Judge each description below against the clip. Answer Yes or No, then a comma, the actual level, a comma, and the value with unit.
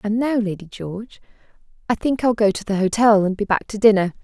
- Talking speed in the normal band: No, fast, 225 wpm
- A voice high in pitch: Yes, high, 210 Hz